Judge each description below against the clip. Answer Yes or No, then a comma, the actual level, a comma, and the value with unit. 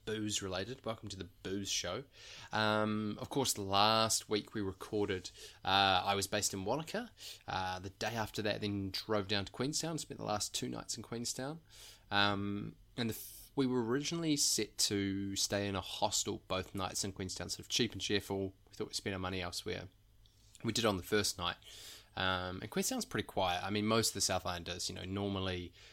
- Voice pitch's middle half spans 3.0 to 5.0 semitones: No, narrow, 2.4 semitones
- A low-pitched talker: Yes, low, 105 Hz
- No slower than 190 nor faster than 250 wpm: Yes, average, 200 wpm